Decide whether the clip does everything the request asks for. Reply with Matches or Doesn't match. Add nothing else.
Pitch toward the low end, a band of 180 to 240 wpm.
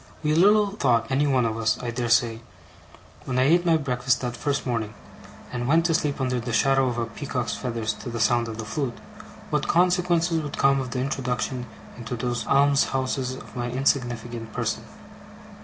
Matches